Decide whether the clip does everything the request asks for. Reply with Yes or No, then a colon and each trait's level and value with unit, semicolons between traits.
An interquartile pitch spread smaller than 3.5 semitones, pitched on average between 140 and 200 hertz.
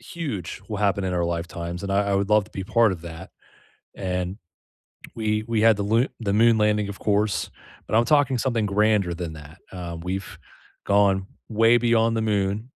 No: average, 3.1 semitones; low, 100 Hz